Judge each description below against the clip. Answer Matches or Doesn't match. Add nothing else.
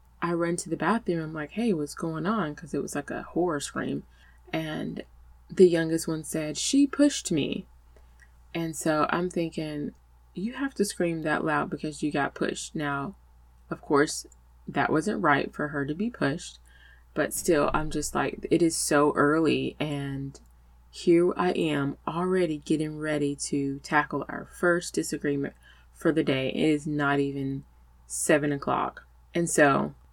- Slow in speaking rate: Doesn't match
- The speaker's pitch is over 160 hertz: Doesn't match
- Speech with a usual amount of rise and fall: Doesn't match